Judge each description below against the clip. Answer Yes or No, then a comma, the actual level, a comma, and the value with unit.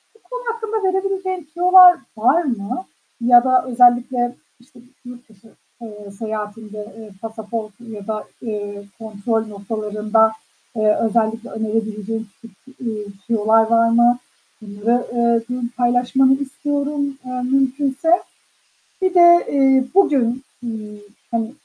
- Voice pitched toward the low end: No, high, 235 Hz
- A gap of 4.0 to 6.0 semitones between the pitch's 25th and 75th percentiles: No, average, 3.5 semitones